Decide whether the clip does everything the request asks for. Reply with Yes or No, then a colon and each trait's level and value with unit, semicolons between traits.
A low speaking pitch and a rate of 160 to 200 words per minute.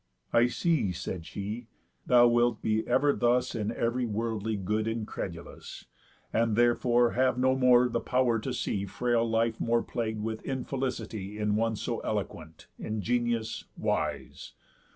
No: low, 115 Hz; average, 140 wpm